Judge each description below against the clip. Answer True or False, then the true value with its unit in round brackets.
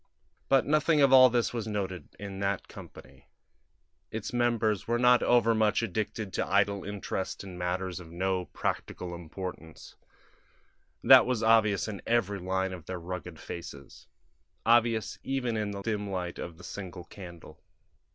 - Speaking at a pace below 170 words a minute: True (150 wpm)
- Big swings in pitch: False (3.9 semitones)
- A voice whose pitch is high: False (100 Hz)